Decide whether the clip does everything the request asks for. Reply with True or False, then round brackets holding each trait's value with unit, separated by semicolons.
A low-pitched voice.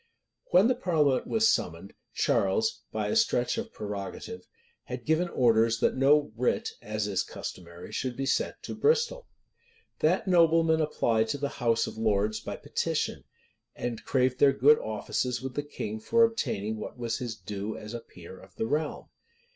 True (130 Hz)